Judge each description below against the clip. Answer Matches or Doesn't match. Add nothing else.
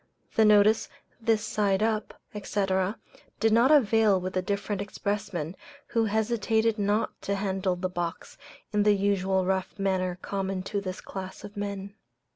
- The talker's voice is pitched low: Doesn't match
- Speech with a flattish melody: Matches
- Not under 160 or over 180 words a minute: Doesn't match